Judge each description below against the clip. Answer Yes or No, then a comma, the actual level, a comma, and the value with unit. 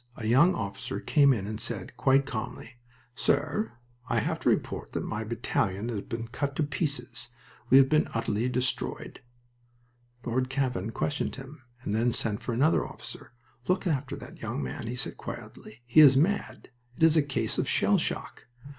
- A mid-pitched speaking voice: No, low, 125 Hz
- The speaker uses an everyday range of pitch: Yes, average, 3.7 semitones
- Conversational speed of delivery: Yes, average, 175 wpm